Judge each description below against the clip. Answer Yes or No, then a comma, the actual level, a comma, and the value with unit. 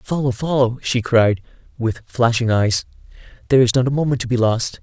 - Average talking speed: Yes, average, 185 wpm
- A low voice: Yes, low, 120 Hz